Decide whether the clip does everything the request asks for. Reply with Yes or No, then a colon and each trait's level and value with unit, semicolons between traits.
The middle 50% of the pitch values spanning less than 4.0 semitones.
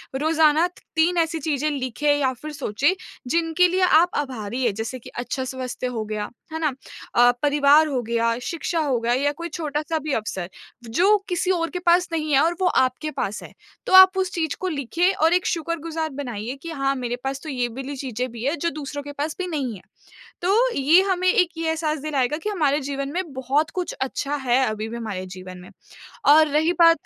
No: average, 4.7 semitones